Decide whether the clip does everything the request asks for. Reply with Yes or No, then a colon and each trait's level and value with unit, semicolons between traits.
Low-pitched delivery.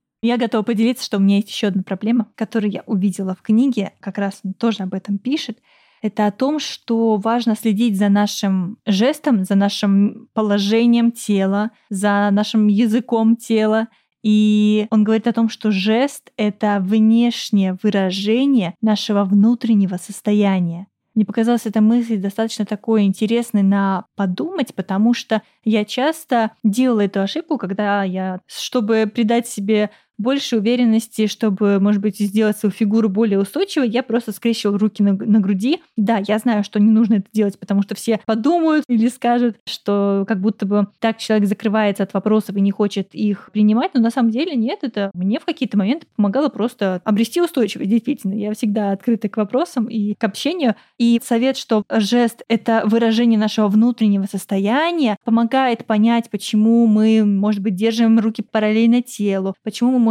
No: high, 220 Hz